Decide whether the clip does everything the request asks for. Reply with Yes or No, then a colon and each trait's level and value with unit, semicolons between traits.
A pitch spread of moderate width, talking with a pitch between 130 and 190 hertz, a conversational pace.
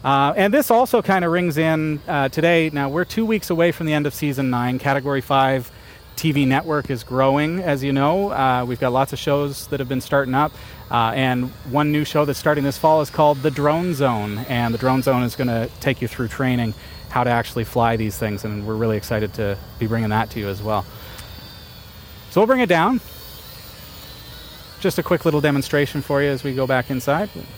No: average, 4.3 semitones; low, 135 Hz; fast, 220 wpm